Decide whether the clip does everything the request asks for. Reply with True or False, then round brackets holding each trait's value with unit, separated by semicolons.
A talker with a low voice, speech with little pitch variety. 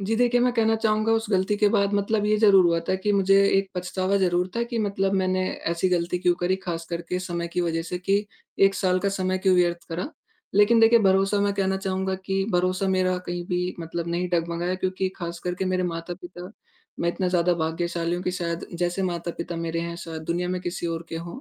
False (185 Hz; 2.2 semitones)